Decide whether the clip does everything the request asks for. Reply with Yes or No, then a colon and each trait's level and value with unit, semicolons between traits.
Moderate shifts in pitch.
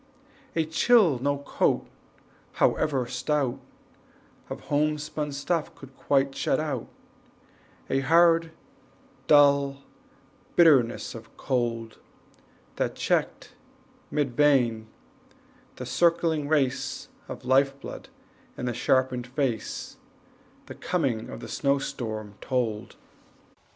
Yes: average, 3.4 semitones